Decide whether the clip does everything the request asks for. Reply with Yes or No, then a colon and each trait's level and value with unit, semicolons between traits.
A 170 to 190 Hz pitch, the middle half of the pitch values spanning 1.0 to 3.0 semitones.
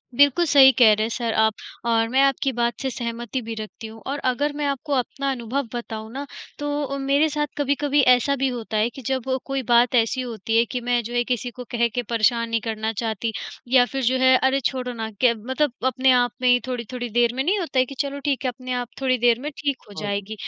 No: very high, 250 Hz; average, 2.7 semitones